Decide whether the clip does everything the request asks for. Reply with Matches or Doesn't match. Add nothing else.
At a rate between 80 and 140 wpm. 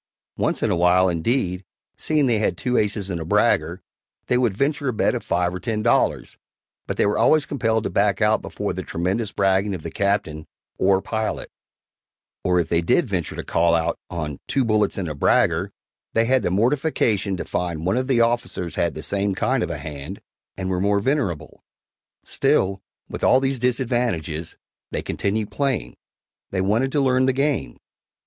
Doesn't match